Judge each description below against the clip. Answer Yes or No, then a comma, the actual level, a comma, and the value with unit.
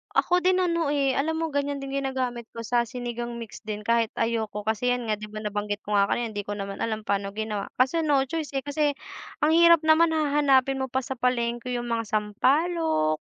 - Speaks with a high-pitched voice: Yes, high, 245 Hz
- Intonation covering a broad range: No, average, 5.0 semitones